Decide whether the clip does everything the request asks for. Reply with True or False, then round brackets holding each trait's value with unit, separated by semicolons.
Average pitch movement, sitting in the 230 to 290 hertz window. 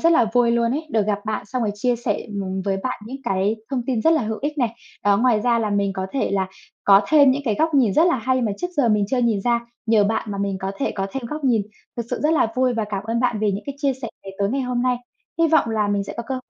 True (4.1 semitones; 235 Hz)